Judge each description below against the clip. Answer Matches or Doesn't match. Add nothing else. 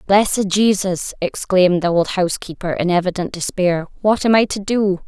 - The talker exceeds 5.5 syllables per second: Doesn't match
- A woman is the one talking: Matches